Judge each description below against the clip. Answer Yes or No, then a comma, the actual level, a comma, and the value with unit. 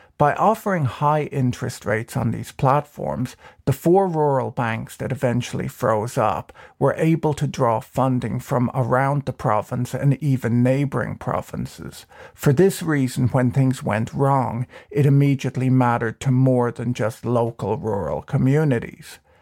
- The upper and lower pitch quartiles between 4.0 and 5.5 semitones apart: No, average, 2.7 semitones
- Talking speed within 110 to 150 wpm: Yes, average, 140 wpm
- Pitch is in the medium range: No, low, 130 Hz